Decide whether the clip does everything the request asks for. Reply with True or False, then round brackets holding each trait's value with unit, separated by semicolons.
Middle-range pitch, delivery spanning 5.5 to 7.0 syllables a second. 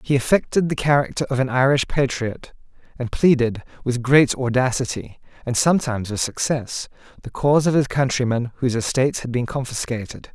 False (130 Hz; 5.7 syllables/s)